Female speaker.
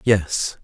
No: male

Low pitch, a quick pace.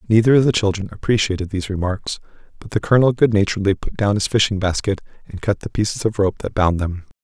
Yes: low, 100 Hz; fast, 215 wpm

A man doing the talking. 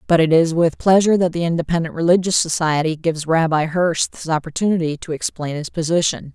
No: female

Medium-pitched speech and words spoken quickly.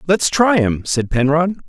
No: medium, 160 Hz; average, 180 wpm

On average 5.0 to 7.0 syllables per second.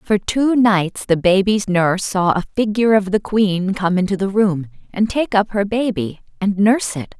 No: 4.6 syllables/s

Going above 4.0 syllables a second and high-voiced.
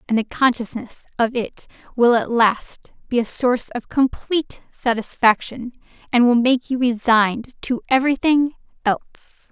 Yes: 4.5 syllables/s; high, 240 Hz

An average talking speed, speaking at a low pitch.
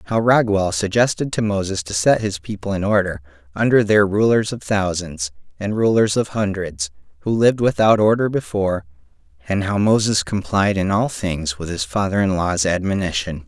Yes: average, 170 wpm; low, 100 Hz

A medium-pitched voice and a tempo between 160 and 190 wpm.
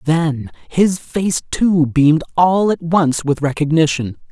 No: medium, 160 Hz; average, 140 wpm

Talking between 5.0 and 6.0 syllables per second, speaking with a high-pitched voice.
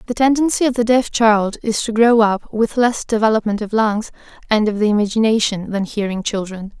Yes: 5.4 syllables/s; high, 220 Hz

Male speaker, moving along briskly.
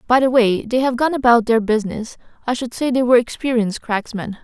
No: female; fast, 215 wpm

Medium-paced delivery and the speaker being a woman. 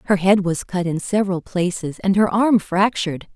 Yes: average, 195 wpm; female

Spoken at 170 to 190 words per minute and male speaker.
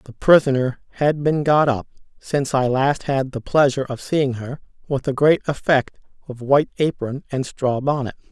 Yes: average, 180 wpm; male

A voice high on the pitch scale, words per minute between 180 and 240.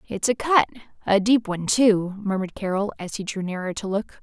Yes: high, 205 Hz; average, 200 wpm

